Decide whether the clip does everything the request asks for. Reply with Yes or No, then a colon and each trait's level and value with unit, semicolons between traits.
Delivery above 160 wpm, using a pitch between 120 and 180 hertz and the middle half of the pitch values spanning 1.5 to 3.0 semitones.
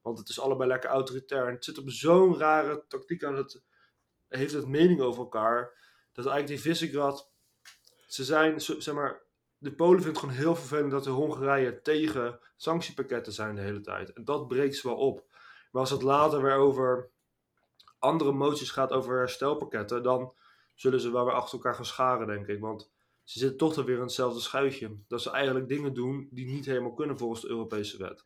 Yes: fast, 200 wpm; low, 135 Hz; narrow, 2.5 semitones